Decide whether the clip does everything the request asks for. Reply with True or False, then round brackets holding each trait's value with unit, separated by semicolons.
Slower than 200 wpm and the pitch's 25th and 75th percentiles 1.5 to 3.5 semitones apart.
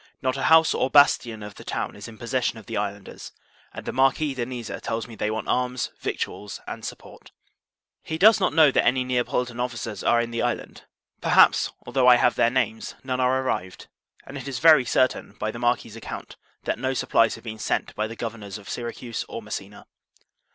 False (205 wpm; 2.7 semitones)